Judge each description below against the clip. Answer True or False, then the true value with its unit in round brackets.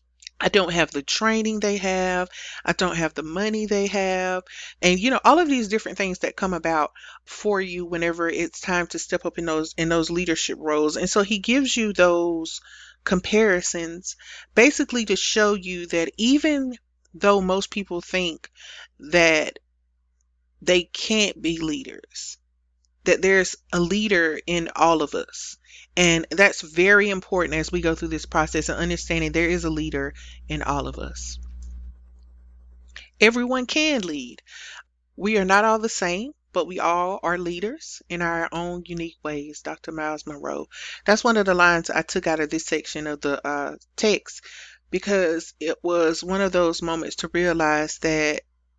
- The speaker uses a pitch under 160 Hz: False (175 Hz)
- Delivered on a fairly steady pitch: False (4.1 semitones)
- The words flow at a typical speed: True (165 wpm)